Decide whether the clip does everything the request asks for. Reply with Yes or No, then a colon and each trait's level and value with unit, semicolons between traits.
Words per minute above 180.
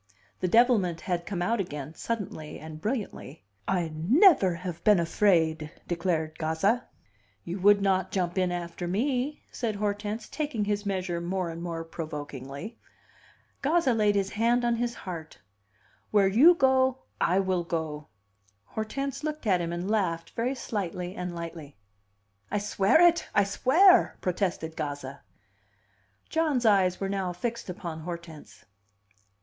No: average, 140 wpm